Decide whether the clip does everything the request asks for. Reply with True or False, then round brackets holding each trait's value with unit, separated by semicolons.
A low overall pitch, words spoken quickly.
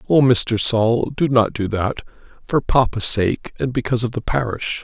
False (120 Hz; 175 wpm)